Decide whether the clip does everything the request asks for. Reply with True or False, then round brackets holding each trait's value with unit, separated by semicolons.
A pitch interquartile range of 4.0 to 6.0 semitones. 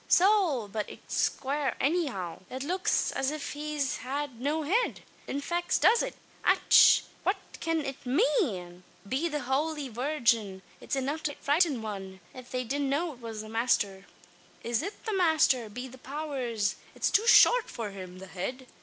True (5.6 semitones)